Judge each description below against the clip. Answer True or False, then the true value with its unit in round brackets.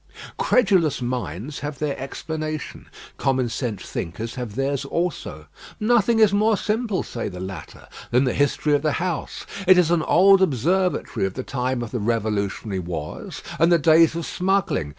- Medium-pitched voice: True (145 Hz)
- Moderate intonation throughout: False (7.3 semitones)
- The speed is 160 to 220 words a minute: True (165 wpm)